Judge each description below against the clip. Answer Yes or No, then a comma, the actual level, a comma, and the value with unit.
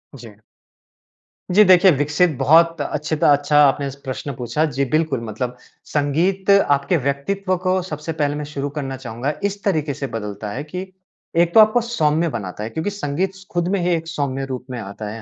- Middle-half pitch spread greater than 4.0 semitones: Yes, average, 4.9 semitones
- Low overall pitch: No, medium, 150 Hz